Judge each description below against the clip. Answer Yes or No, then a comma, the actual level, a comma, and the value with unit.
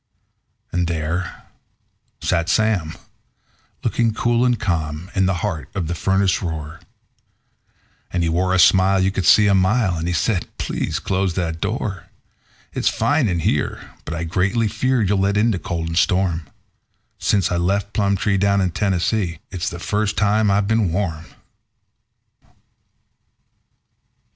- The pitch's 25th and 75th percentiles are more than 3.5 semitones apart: No, average, 3.2 semitones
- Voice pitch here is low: Yes, very low, 95 Hz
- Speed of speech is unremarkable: Yes, average, 150 wpm